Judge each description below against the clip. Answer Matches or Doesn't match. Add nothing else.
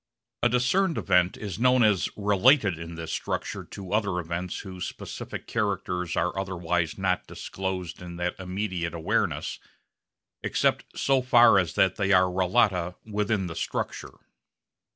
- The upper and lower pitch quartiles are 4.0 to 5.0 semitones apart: Doesn't match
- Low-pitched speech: Matches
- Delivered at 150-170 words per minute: Doesn't match